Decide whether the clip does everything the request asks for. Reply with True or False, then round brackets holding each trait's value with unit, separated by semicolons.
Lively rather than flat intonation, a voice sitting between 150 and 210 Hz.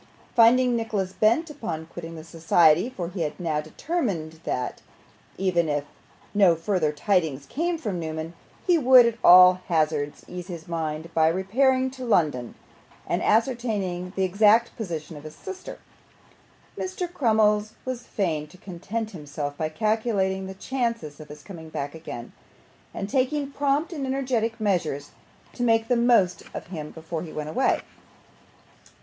True (6.6 semitones; 190 Hz)